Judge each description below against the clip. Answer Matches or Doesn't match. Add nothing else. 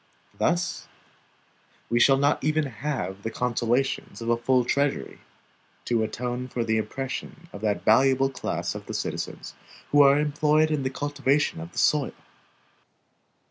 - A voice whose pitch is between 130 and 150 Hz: Matches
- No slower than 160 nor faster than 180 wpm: Doesn't match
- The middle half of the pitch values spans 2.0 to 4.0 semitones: Matches